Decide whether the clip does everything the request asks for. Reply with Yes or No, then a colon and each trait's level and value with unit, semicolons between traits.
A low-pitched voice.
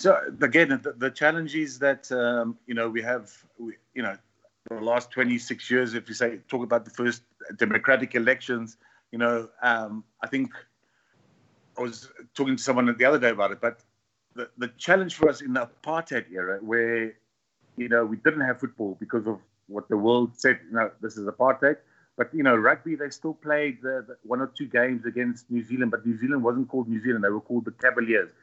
Yes: low, 120 Hz